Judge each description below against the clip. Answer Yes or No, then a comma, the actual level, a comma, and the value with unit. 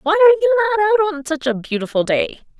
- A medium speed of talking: No, fast, 230 wpm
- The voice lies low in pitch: No, very high, 305 Hz